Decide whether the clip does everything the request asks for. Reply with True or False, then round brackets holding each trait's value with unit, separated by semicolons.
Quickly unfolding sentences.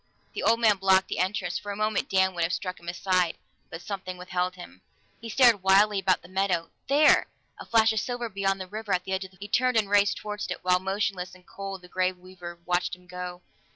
True (240 wpm)